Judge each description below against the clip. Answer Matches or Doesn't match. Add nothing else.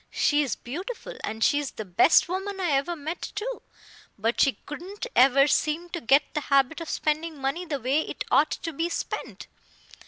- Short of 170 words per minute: Doesn't match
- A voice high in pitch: Matches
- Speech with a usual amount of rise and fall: Matches